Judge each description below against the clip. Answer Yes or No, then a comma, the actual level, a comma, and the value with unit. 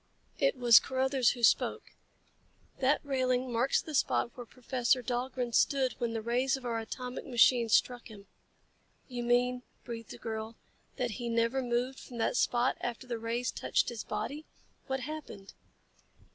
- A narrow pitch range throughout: Yes, narrow, 1.8 semitones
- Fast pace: No, average, 160 wpm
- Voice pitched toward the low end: No, high, 245 Hz